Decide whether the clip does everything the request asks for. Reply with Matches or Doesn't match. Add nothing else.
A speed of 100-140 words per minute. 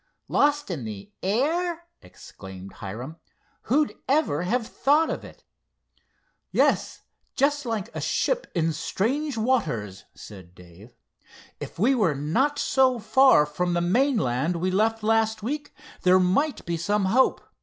Matches